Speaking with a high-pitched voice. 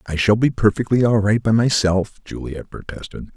No: low, 105 Hz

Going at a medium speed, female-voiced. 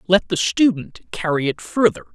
No: average, 170 wpm; male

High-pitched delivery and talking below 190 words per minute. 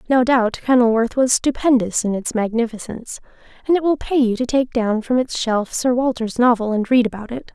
No: high, 240 Hz; fast, 205 wpm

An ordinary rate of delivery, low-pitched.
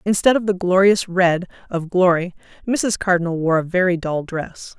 No: average, 175 wpm; medium, 180 Hz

